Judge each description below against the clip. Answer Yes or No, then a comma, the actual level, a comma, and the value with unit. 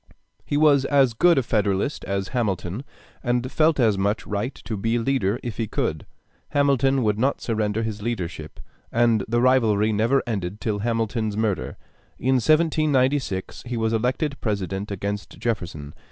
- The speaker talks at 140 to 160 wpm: Yes, average, 155 wpm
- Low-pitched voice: Yes, low, 115 Hz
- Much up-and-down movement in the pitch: No, average, 4.2 semitones